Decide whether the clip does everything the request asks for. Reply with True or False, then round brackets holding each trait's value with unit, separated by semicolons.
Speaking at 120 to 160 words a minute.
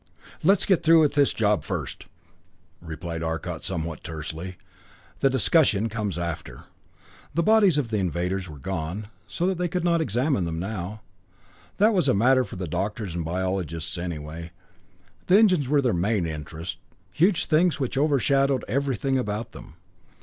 True (155 wpm)